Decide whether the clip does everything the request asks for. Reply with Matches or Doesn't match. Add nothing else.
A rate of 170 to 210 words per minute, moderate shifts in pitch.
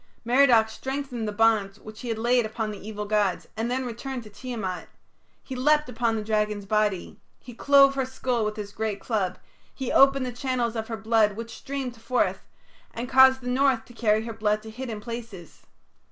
Matches